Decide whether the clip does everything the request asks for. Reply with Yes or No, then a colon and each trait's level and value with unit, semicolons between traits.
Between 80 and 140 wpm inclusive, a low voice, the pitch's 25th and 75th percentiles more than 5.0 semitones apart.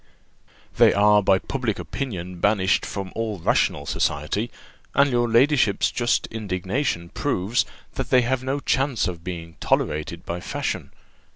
Yes: slow, 135 wpm; low, 105 Hz; wide, 5.4 semitones